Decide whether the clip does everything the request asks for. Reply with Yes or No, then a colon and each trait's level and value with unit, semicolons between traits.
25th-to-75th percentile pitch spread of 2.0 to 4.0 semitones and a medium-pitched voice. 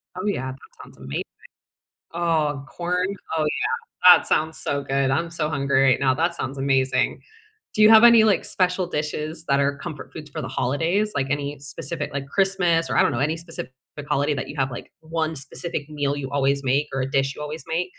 Yes: average, 3.5 semitones; medium, 150 Hz